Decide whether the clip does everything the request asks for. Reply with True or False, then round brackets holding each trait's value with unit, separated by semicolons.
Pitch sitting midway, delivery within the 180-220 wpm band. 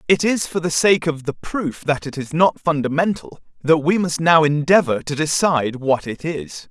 True (155 Hz; 205 wpm)